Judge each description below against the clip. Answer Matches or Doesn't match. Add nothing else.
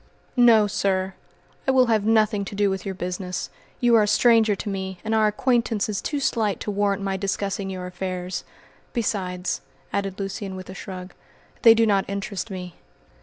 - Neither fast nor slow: Matches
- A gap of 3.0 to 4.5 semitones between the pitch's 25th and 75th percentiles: Doesn't match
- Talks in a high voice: Matches